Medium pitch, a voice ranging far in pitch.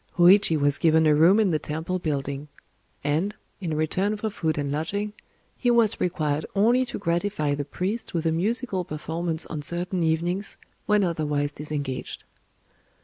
No: medium, 165 Hz; average, 4.7 semitones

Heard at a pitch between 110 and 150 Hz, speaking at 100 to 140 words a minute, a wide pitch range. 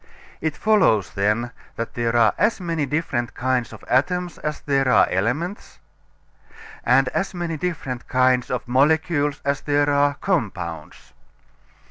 No: medium, 140 Hz; slow, 135 wpm; average, 4.8 semitones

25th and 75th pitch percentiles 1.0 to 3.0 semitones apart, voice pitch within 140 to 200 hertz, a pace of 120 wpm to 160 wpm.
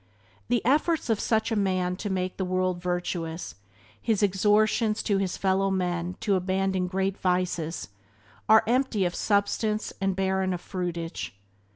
Yes: narrow, 2.5 semitones; high, 190 Hz; average, 150 wpm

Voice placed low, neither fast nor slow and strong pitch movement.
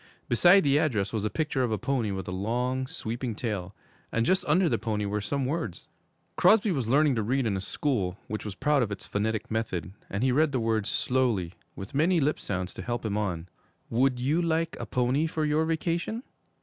No: low, 125 Hz; fast, 215 wpm; wide, 6.2 semitones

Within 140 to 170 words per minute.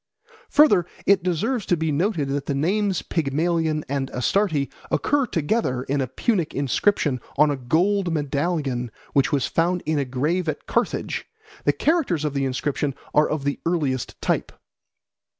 Yes: average, 155 wpm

